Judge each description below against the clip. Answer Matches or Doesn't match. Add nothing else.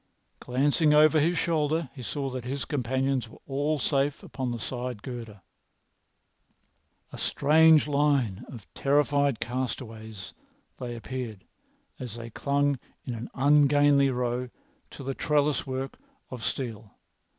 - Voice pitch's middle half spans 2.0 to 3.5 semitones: Matches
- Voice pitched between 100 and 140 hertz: Matches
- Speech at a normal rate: Doesn't match